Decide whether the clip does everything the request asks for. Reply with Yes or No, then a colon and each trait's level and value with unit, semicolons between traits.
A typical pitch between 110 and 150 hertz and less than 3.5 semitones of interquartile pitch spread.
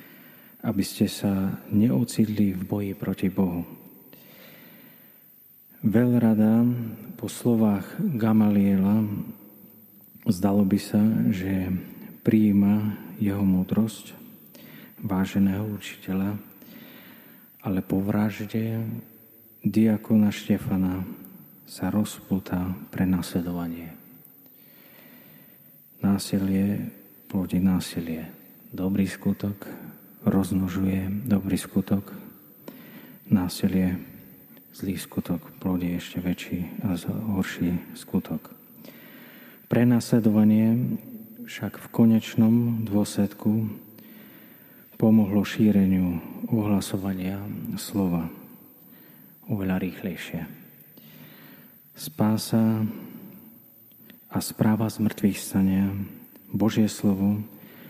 No: low, 100 Hz; narrow, 2.4 semitones